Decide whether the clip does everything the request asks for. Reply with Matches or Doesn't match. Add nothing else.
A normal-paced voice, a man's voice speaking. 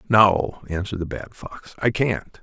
Matches